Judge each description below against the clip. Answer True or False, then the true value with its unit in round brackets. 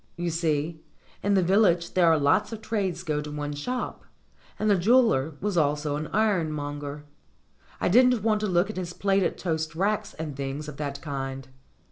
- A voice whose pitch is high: False (170 Hz)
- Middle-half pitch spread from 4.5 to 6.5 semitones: True (5.4 semitones)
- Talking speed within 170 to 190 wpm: True (180 wpm)